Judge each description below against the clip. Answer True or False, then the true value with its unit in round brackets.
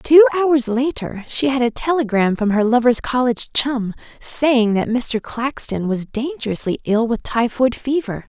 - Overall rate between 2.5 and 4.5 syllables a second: True (4.4 syllables/s)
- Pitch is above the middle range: True (245 Hz)